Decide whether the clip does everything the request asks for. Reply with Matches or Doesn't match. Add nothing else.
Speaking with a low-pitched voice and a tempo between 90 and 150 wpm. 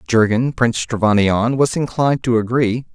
Matches